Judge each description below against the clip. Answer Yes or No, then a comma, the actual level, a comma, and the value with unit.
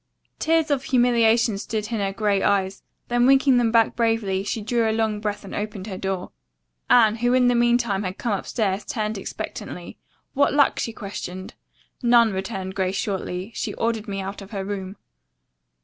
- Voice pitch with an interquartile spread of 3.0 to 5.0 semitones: Yes, average, 3.4 semitones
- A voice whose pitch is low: No, high, 215 Hz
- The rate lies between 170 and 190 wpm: Yes, average, 180 wpm